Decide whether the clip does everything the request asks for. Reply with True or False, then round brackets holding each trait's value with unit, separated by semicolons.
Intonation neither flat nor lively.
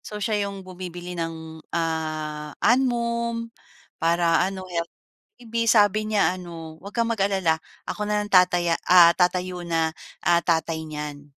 True (4.0 semitones)